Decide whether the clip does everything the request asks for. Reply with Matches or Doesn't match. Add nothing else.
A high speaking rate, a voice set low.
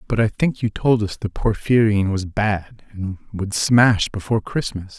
Doesn't match